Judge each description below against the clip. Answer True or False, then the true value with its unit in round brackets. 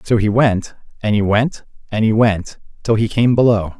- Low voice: True (110 Hz)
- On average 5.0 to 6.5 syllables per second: False (4.7 syllables/s)